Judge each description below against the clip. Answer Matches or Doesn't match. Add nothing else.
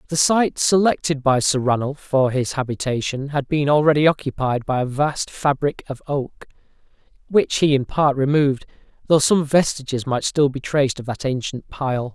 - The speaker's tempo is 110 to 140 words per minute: Doesn't match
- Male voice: Matches